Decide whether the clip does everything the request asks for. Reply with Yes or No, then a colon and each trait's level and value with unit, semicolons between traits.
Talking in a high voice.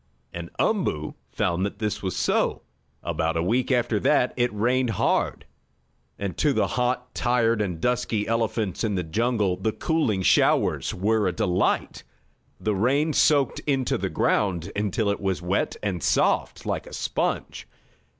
No: low, 105 Hz